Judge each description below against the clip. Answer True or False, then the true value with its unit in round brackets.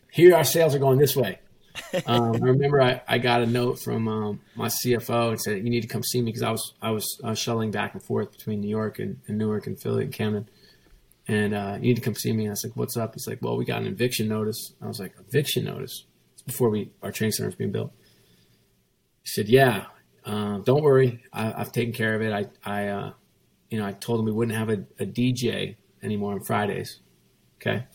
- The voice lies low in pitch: True (110 Hz)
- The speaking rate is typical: False (240 wpm)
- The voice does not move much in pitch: False (3.0 semitones)